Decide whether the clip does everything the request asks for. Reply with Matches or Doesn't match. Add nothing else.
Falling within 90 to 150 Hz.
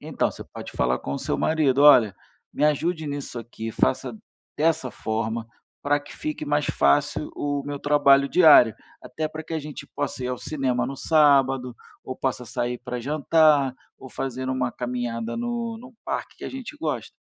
Matches